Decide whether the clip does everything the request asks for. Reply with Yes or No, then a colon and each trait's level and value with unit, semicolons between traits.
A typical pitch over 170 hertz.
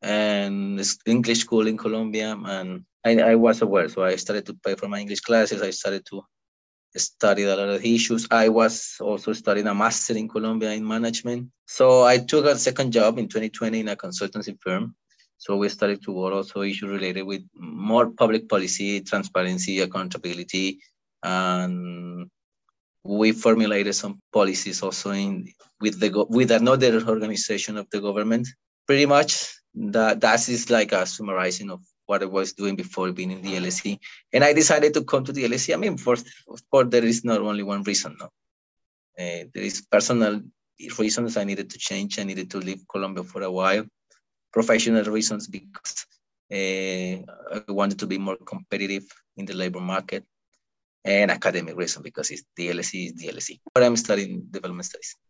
No: low, 105 Hz